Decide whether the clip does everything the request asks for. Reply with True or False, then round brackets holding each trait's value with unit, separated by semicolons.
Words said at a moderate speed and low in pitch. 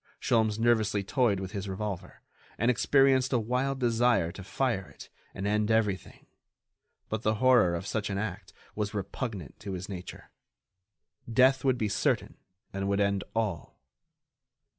True (150 wpm; 105 Hz)